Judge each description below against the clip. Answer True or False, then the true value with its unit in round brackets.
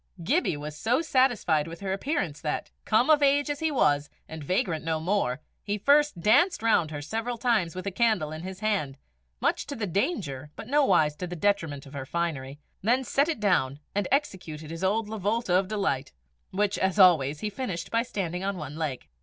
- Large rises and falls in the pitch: True (6.6 semitones)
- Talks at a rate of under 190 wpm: False (200 wpm)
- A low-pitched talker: False (190 Hz)